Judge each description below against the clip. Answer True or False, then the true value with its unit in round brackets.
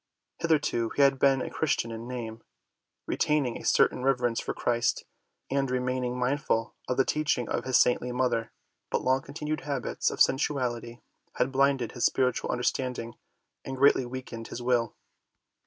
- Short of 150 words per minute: False (155 wpm)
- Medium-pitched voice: False (125 Hz)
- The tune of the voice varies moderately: False (2.1 semitones)